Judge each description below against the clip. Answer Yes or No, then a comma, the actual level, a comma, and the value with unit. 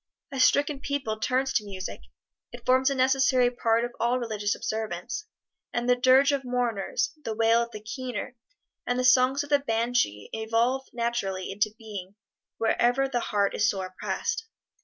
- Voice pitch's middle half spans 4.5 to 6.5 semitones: No, average, 3.2 semitones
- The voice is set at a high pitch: Yes, high, 240 Hz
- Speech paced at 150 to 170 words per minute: Yes, average, 165 wpm